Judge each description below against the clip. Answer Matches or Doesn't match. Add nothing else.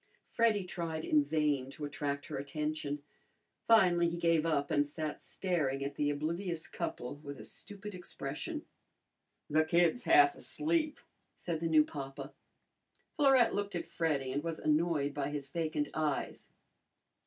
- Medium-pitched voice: Matches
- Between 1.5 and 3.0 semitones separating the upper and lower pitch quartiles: Doesn't match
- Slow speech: Doesn't match